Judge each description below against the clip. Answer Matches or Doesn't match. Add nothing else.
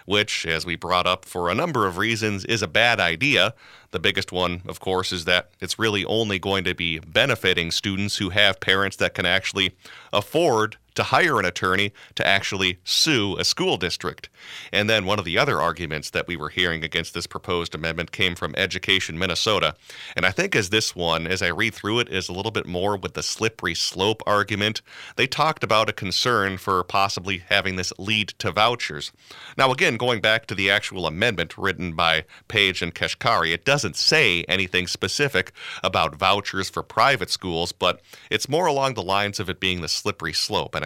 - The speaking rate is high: Doesn't match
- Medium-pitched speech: Doesn't match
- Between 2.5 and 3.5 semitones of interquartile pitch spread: Matches